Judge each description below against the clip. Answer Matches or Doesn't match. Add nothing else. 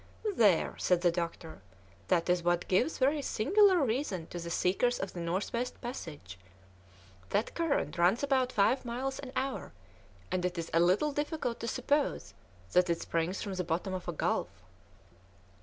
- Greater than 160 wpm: Matches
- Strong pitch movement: Matches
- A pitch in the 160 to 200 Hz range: Matches